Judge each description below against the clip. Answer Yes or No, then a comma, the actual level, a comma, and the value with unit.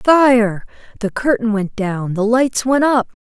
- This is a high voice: Yes, high, 230 Hz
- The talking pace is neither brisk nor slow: Yes, average, 150 wpm